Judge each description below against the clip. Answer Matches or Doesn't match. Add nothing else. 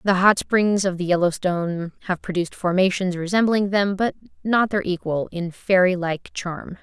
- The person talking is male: Doesn't match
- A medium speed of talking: Matches